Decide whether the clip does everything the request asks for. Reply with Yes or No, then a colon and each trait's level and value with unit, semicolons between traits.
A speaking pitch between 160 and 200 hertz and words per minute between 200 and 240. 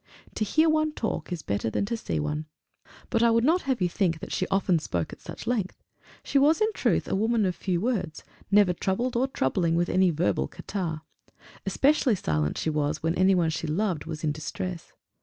Yes: medium, 185 Hz; fast, 205 wpm